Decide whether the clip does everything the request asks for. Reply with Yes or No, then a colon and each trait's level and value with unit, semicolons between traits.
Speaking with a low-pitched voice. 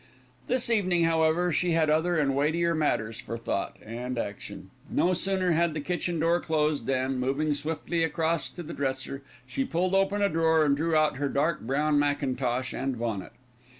No: medium, 155 Hz